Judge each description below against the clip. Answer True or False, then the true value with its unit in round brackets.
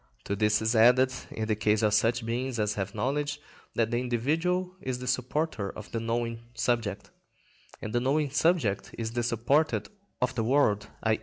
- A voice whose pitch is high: False (120 Hz)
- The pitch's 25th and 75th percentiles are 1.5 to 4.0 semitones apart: True (3.2 semitones)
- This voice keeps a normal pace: True (180 wpm)